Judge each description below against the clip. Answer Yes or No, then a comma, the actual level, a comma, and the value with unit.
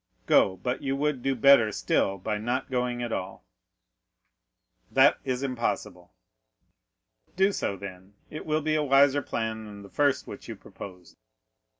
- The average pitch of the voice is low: Yes, low, 120 Hz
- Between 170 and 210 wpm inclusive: No, average, 155 wpm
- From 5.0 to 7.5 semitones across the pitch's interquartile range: Yes, wide, 5.5 semitones